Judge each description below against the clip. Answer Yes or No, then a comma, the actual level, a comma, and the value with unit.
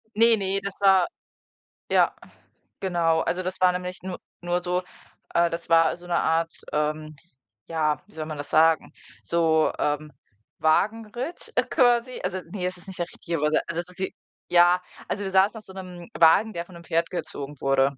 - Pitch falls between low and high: Yes, medium, 175 Hz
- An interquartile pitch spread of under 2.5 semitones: No, average, 2.8 semitones